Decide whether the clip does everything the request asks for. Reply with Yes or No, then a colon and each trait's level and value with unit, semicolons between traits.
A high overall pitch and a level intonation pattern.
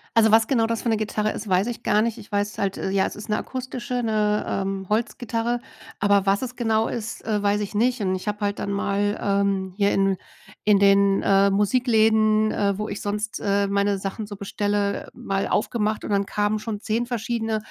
Yes: high, 210 Hz; narrow, 1.9 semitones